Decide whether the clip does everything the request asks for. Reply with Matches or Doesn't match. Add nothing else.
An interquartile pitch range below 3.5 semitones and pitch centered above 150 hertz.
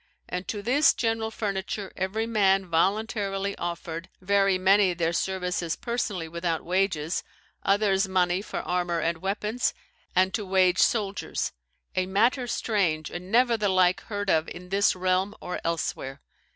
Matches